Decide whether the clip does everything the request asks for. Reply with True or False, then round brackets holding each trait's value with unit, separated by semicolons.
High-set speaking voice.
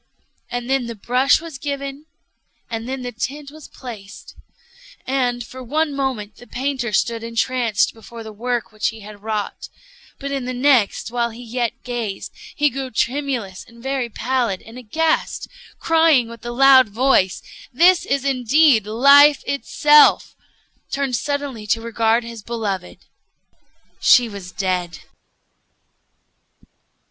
True (245 Hz)